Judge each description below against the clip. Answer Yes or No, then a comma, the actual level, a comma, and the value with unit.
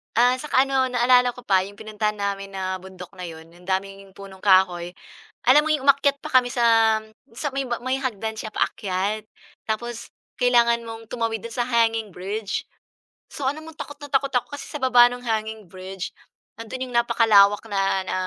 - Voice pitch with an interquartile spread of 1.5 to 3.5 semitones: No, average, 4.1 semitones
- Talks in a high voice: Yes, high, 225 Hz